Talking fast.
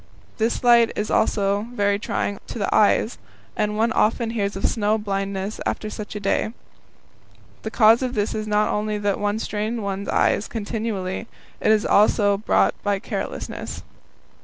No: average, 165 wpm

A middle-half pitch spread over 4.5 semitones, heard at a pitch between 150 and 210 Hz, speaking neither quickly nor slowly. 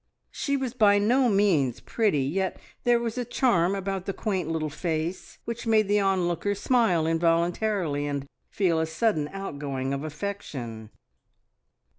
Yes: wide, 5.4 semitones; medium, 185 Hz; average, 145 wpm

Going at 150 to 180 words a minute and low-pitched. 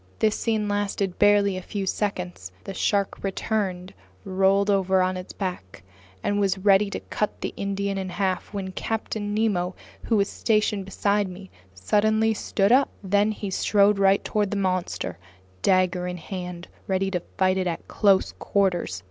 No: average, 165 wpm; high, 195 Hz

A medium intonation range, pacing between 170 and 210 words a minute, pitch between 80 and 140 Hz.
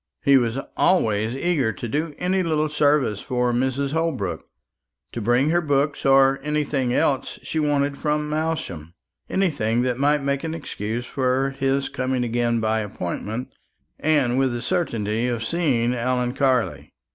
No: average, 3.9 semitones; average, 150 wpm; low, 135 Hz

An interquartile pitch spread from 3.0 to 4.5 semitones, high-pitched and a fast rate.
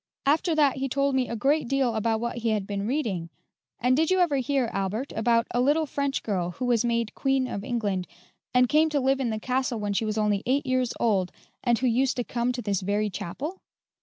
Yes: average, 4.0 semitones; high, 245 Hz; fast, 230 wpm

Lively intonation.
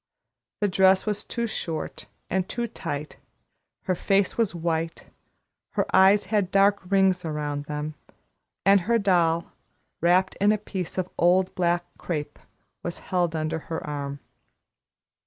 No: average, 3.3 semitones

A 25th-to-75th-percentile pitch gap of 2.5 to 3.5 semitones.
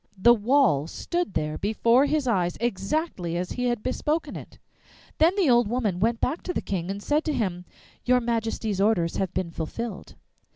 No: wide, 5.4 semitones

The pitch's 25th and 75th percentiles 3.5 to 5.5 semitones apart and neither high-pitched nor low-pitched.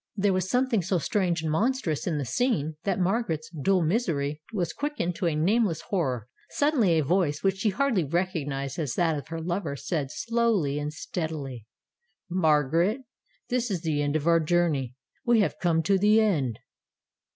Yes: average, 5.0 semitones; medium, 170 Hz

